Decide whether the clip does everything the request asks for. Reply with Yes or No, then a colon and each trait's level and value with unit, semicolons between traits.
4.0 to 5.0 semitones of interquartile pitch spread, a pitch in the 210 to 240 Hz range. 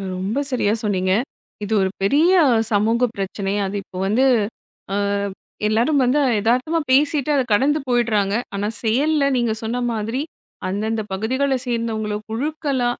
Yes: average, 4.4 semitones; high, 230 Hz